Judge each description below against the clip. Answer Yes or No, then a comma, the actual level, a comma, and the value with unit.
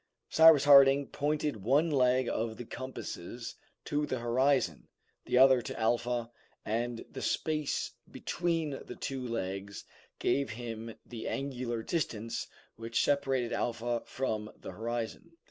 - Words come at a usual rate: No, slow, 130 wpm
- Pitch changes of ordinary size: Yes, average, 3.3 semitones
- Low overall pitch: Yes, low, 125 Hz